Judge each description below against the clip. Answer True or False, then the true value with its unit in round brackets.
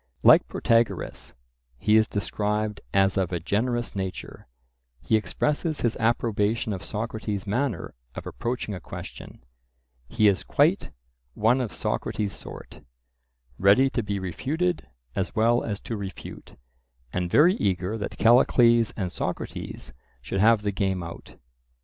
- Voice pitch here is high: False (105 Hz)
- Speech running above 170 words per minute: False (135 wpm)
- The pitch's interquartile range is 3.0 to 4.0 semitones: True (3.3 semitones)